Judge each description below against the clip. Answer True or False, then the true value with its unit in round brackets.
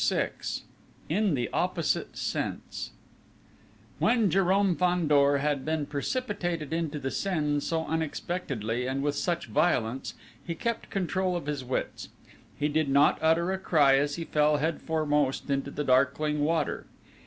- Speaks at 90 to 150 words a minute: True (140 wpm)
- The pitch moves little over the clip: False (3.6 semitones)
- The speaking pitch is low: False (150 Hz)